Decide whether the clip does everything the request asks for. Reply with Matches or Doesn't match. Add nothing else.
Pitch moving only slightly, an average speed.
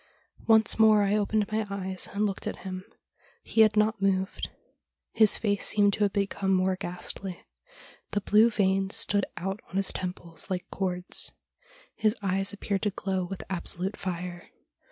Matches